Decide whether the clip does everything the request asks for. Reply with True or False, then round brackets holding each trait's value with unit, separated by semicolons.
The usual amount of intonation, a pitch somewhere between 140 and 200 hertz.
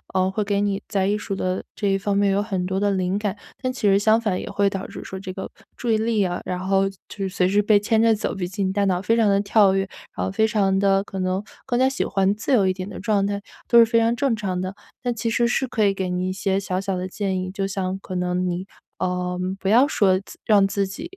False (2.1 semitones; 195 Hz)